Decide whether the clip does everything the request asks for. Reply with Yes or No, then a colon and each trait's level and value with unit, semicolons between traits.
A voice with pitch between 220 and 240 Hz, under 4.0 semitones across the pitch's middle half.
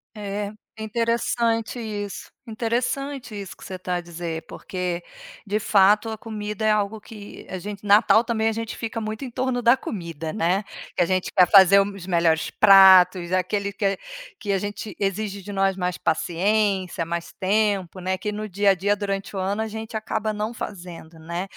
No: high, 200 Hz; average, 2.8 semitones